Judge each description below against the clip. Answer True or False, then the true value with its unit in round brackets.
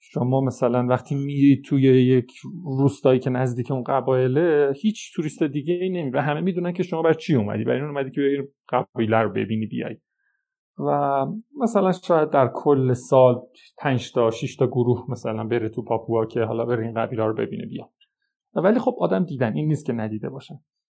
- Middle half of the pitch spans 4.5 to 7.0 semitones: True (5.0 semitones)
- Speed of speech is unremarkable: False (185 wpm)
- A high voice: False (135 Hz)